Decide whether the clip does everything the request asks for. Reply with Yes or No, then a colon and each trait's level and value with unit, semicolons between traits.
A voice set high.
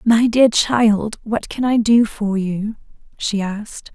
Yes: high, 220 Hz